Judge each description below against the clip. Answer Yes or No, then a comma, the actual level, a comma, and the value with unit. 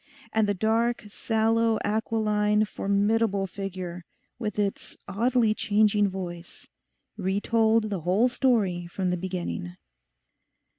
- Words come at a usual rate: No, slow, 110 wpm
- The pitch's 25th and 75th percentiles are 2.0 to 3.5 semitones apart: Yes, average, 2.9 semitones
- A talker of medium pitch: No, high, 210 Hz